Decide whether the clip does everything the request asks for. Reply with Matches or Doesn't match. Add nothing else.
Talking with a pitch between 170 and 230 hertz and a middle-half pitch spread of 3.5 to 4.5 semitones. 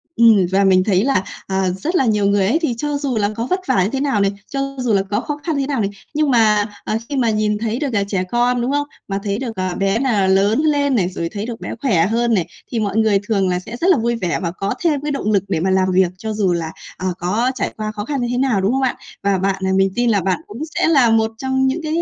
Doesn't match